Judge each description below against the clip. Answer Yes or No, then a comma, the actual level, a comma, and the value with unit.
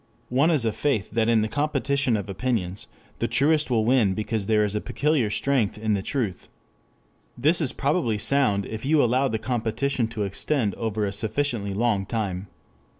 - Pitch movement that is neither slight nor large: Yes, average, 4.8 semitones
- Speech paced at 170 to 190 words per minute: Yes, average, 180 wpm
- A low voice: Yes, low, 115 Hz